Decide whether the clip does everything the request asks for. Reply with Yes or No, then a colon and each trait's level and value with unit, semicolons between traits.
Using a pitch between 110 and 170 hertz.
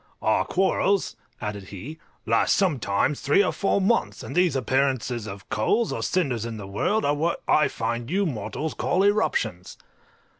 Yes: medium, 140 Hz